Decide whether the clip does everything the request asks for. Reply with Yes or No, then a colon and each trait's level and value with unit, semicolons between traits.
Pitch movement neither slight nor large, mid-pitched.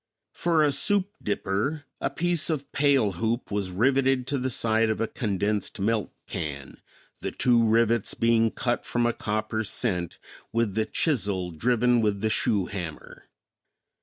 No: average, 4.1 semitones; low, 115 Hz